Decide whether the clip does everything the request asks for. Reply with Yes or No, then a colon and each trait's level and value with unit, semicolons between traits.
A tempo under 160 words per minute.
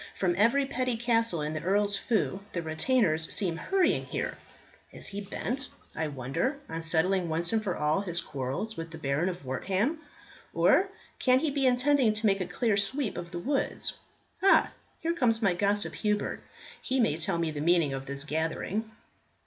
No: average, 180 wpm